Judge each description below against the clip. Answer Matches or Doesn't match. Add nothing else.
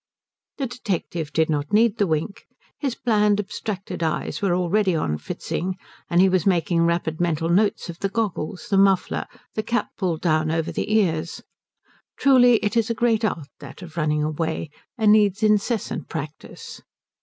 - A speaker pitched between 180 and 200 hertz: Matches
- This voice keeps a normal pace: Matches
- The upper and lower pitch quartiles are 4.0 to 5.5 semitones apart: Matches